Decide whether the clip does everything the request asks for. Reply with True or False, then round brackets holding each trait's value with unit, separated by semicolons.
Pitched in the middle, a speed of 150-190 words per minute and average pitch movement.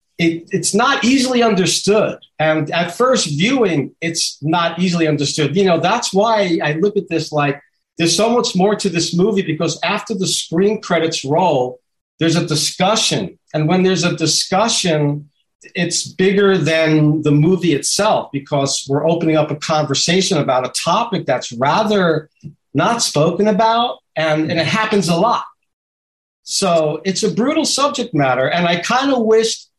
True (170 Hz; 160 wpm; 4.9 semitones)